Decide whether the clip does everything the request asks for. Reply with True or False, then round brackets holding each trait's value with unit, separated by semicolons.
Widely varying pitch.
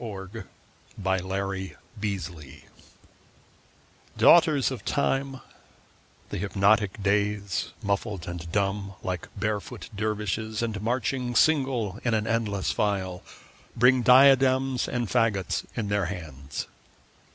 False (3.9 semitones)